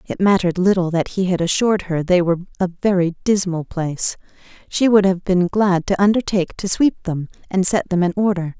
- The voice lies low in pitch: No, medium, 185 Hz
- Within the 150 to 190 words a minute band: No, average, 200 wpm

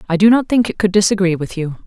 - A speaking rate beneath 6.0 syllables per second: No, 6.6 syllables/s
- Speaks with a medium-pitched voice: No, high, 195 Hz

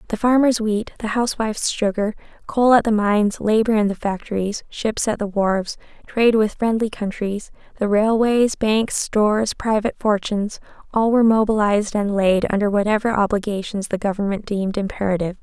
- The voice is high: Yes, high, 210 Hz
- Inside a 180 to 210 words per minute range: No, average, 150 wpm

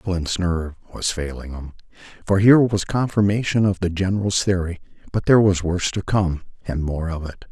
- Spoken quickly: No, average, 185 wpm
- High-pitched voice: No, very low, 90 Hz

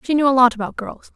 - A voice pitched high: Yes, very high, 255 Hz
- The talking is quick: Yes, fast, 310 wpm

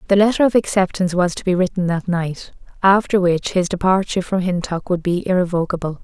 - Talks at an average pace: Yes, average, 190 wpm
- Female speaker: Yes, female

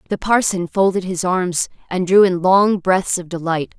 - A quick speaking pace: No, average, 190 wpm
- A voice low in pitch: No, medium, 185 Hz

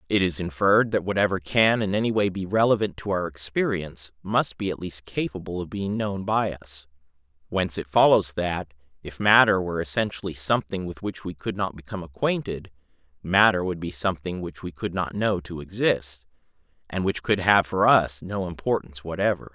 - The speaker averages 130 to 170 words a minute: No, average, 185 wpm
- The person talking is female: No, male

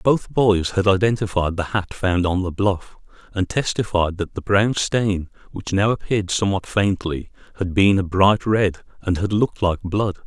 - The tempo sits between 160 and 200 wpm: Yes, average, 180 wpm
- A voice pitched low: Yes, very low, 95 Hz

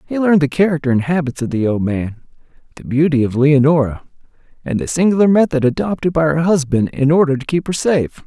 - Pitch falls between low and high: Yes, medium, 145 Hz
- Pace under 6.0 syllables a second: No, 6.2 syllables/s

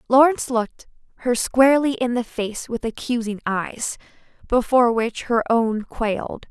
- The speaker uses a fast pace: No, average, 140 wpm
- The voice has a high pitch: Yes, high, 235 Hz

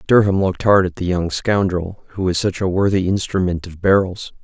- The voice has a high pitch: No, very low, 95 Hz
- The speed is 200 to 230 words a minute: Yes, fast, 205 wpm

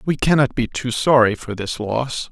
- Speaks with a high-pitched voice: No, low, 120 Hz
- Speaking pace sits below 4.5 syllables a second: No, 4.6 syllables/s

